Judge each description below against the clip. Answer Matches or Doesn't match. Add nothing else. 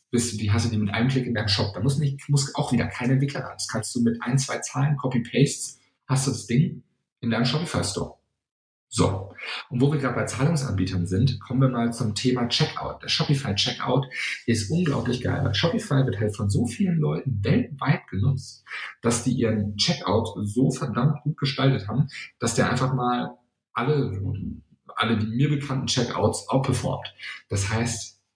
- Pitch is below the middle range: Matches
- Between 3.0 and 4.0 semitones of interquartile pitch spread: Matches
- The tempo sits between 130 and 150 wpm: Doesn't match